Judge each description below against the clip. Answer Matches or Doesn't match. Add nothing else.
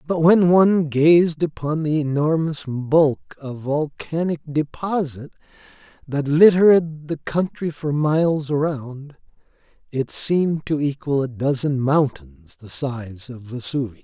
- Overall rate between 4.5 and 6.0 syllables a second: Doesn't match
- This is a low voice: Doesn't match